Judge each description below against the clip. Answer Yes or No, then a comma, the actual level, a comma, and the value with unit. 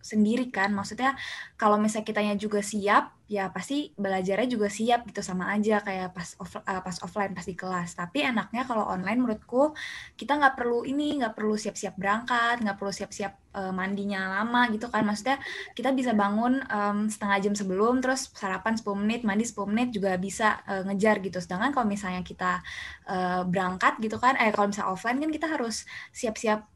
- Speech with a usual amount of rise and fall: Yes, average, 3.4 semitones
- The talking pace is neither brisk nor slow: Yes, average, 180 wpm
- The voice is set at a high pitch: Yes, high, 210 Hz